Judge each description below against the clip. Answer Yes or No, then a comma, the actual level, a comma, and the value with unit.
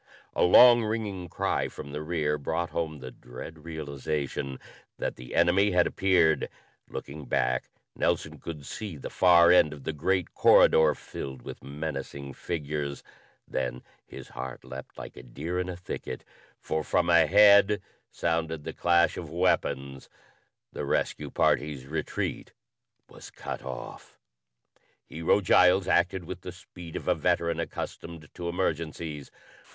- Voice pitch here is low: Yes, very low, 80 Hz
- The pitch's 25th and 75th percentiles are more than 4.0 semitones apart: No, average, 3.7 semitones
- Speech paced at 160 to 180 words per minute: No, average, 140 wpm